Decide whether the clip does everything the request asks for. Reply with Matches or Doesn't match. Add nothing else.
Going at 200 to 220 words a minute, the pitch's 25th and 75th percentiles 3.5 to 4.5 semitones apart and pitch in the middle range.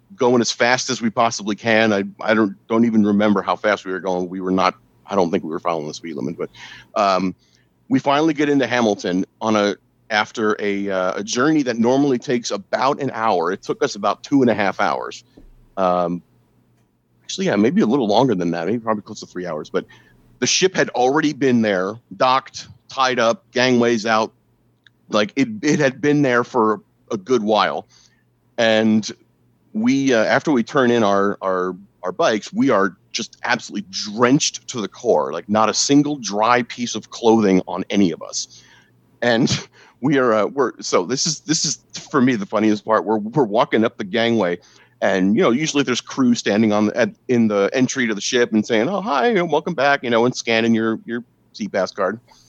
Doesn't match